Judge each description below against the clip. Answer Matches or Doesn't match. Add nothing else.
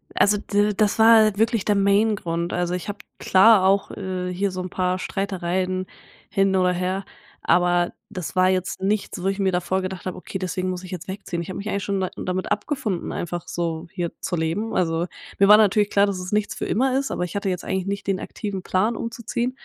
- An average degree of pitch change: Doesn't match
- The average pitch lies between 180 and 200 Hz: Matches